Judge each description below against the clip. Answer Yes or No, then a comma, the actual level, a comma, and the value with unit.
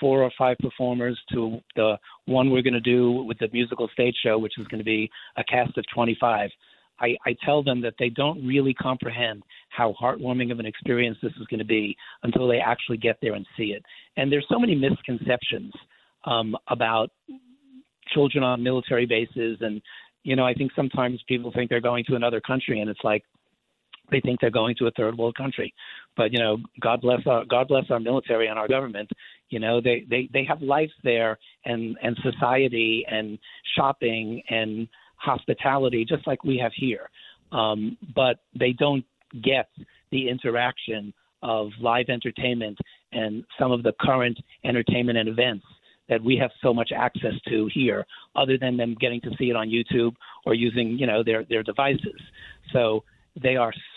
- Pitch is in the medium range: No, low, 120 Hz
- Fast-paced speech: No, average, 185 wpm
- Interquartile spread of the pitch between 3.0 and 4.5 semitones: No, narrow, 2.4 semitones